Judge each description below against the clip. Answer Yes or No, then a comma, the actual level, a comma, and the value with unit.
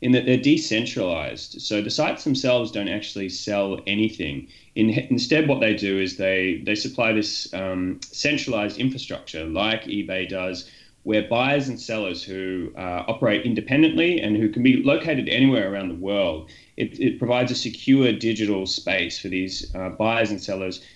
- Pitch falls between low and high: No, low, 110 Hz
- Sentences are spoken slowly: No, average, 165 wpm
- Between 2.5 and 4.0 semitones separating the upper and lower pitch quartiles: No, average, 4.8 semitones